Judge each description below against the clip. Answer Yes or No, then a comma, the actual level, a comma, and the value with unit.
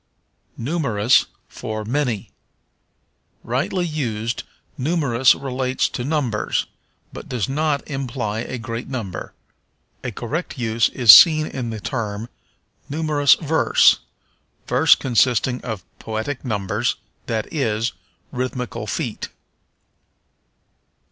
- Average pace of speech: No, slow, 100 wpm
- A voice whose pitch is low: Yes, low, 125 Hz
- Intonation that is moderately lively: Yes, average, 4.2 semitones